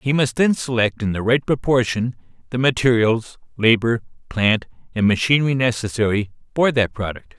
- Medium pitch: No, low, 120 Hz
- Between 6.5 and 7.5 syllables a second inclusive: No, 5.1 syllables/s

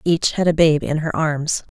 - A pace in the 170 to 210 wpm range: No, fast, 240 wpm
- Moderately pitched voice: Yes, medium, 160 Hz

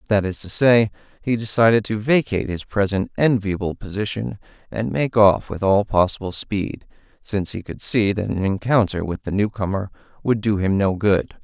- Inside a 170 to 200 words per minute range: Yes, average, 180 wpm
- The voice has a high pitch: No, low, 105 Hz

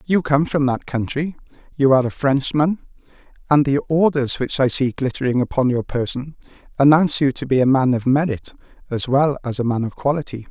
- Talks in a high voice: No, low, 135 Hz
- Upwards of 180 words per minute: Yes, average, 195 wpm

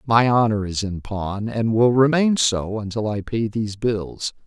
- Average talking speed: Yes, average, 190 wpm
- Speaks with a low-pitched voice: Yes, low, 110 Hz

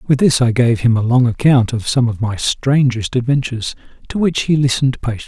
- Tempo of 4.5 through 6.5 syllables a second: Yes, 5.7 syllables/s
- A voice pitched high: No, low, 125 Hz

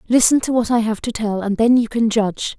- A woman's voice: Yes, female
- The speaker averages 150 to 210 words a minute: No, fast, 280 wpm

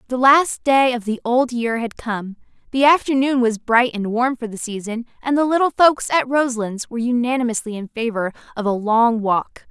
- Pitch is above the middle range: Yes, high, 240 Hz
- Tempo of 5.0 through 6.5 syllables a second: Yes, 5.1 syllables/s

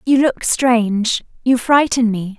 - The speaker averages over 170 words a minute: No, average, 150 wpm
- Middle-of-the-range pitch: No, high, 240 Hz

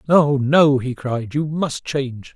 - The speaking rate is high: No, average, 180 wpm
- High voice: No, medium, 140 Hz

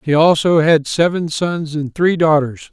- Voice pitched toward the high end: No, medium, 160 Hz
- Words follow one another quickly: No, average, 175 wpm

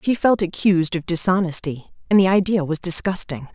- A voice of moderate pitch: Yes, medium, 180 Hz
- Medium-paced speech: Yes, average, 170 wpm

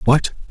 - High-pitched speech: No, low, 135 Hz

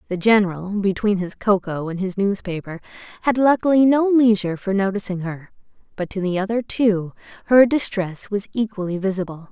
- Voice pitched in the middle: No, high, 200 Hz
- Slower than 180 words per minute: Yes, average, 160 wpm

